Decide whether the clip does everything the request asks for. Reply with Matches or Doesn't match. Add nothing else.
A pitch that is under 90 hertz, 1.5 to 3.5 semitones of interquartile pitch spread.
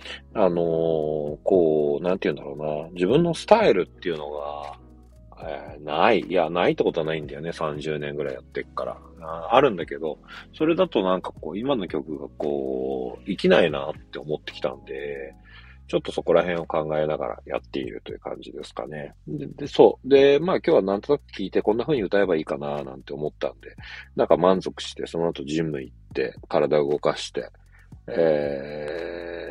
Matches